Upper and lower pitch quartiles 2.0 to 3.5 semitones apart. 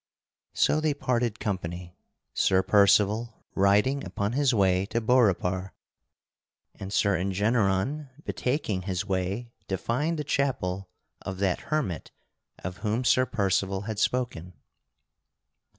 No: average, 4.7 semitones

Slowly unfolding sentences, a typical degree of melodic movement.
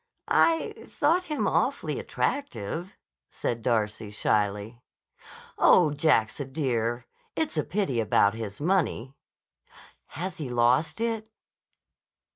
No: slow, 105 wpm; wide, 9.0 semitones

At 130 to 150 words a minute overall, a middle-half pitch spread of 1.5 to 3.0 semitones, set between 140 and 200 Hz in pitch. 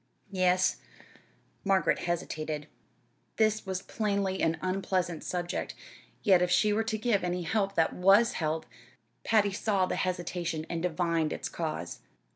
Yes: slow, 135 wpm; average, 2.7 semitones; medium, 185 Hz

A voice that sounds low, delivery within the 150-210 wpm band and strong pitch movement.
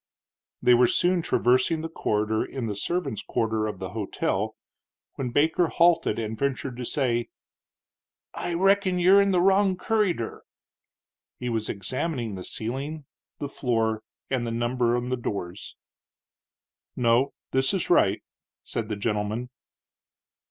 No: low, 125 Hz; average, 140 wpm; wide, 6.8 semitones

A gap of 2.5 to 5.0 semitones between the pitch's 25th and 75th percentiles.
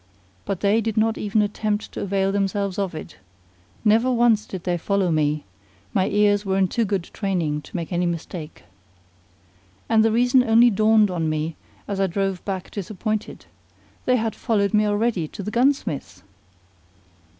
Yes: average, 3.4 semitones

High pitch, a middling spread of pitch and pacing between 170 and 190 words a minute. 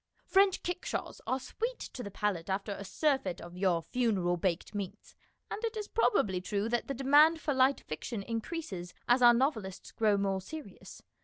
No: high, 225 Hz; wide, 6.9 semitones; average, 175 wpm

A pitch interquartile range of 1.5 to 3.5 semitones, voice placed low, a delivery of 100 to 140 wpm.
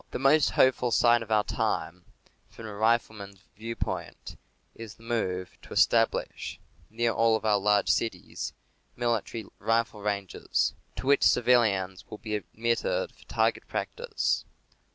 Yes: narrow, 2.4 semitones; low, 115 Hz; slow, 135 wpm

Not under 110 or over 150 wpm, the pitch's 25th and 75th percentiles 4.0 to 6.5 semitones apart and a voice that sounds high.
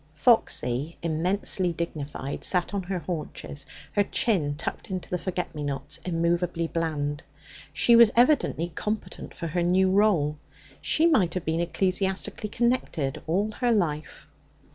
No: average, 140 wpm; average, 4.3 semitones; medium, 175 Hz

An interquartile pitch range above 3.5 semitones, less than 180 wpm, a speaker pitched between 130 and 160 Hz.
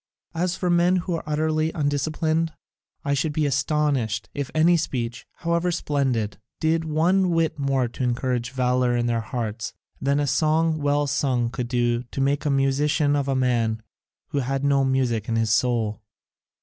Yes: average, 4.2 semitones; average, 170 wpm; medium, 140 Hz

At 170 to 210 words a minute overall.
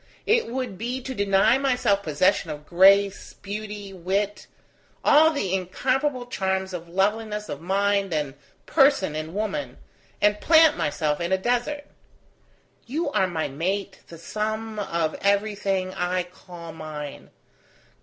No: slow, 135 wpm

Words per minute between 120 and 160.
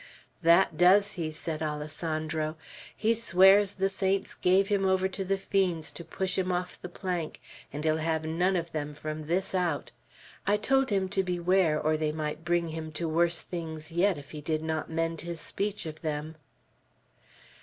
No: average, 180 wpm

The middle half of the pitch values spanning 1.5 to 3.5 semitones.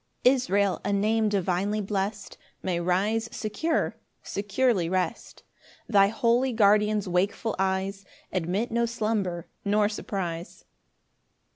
Yes: average, 2.7 semitones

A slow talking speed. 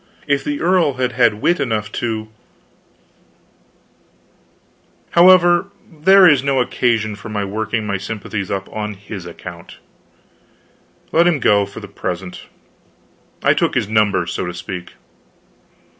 Yes: slow, 130 wpm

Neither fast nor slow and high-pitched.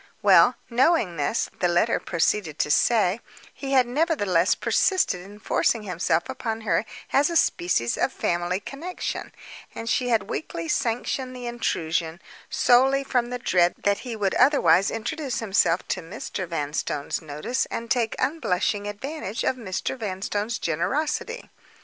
Yes: average, 145 wpm; high, 220 Hz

